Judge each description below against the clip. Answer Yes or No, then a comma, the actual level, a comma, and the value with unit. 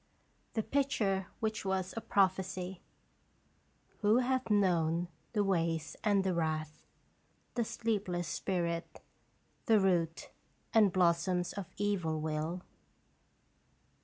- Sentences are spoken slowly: Yes, slow, 105 wpm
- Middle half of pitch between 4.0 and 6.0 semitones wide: No, average, 3.4 semitones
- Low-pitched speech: No, medium, 185 Hz